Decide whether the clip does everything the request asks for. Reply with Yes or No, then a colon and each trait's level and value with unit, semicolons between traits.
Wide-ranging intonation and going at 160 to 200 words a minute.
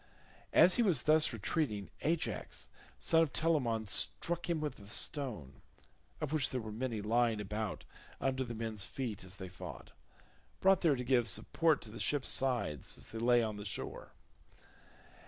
Yes: wide, 6.0 semitones; average, 165 wpm